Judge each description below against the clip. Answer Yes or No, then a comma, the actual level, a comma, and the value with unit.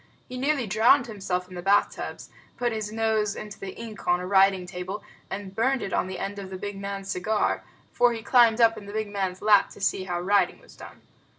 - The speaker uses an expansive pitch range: No, narrow, 2.6 semitones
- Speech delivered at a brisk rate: Yes, fast, 230 wpm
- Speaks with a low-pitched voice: No, high, 205 Hz